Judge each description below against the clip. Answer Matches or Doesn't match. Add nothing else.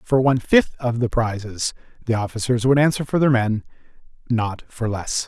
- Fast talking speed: Doesn't match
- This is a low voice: Matches